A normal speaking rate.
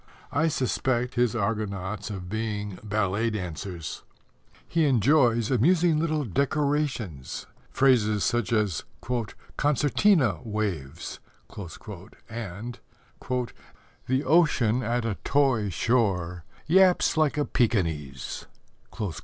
No: slow, 90 wpm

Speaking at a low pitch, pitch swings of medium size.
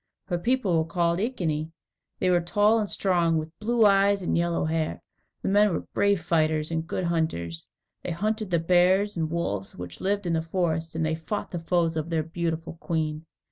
No: medium, 170 Hz; average, 3.1 semitones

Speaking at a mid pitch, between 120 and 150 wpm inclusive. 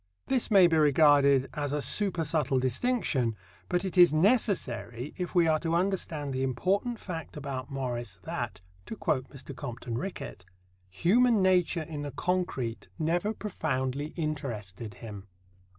Yes: medium, 150 Hz; average, 140 wpm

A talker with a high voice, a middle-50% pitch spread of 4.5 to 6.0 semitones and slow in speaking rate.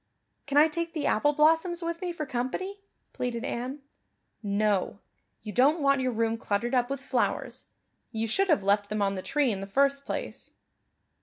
No: very high, 260 Hz; wide, 5.6 semitones; average, 180 wpm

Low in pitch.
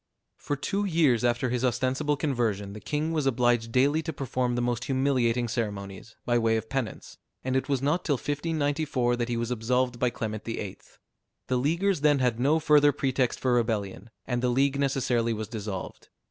Yes: low, 125 Hz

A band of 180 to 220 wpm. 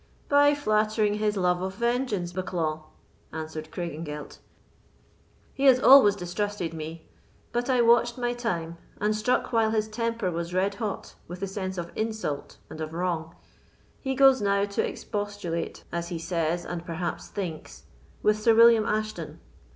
No: average, 150 wpm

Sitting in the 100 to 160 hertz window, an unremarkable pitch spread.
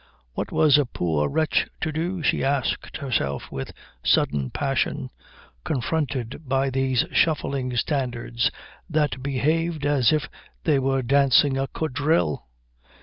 Yes: low, 135 Hz; average, 3.3 semitones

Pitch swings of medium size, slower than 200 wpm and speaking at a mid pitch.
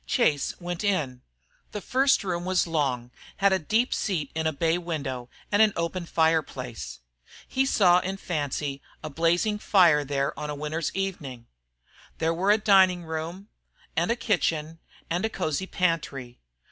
Yes: average, 4.4 semitones; average, 160 wpm; medium, 165 Hz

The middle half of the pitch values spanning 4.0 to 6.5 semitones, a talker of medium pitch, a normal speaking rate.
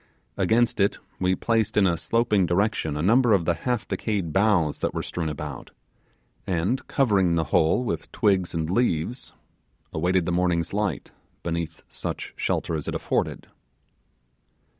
No: average, 4.4 semitones; very low, 90 Hz; average, 150 wpm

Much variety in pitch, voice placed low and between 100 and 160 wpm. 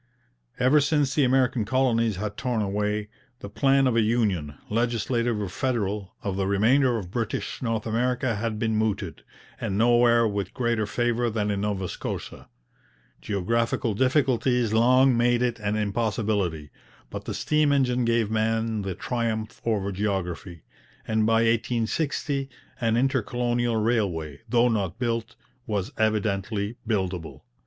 No: average, 2.8 semitones; low, 115 Hz; average, 140 wpm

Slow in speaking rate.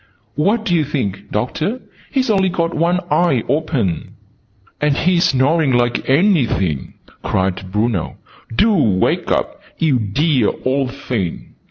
Yes: slow, 130 wpm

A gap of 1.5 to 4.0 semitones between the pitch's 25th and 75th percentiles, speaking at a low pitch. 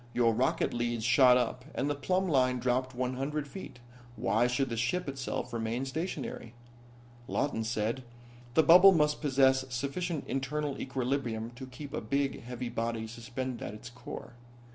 Yes: average, 2.8 semitones; low, 130 Hz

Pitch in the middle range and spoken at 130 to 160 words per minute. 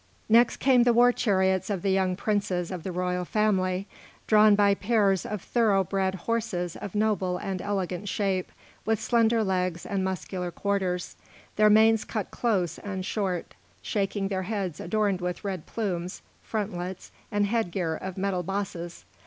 No: high, 195 Hz; average, 155 wpm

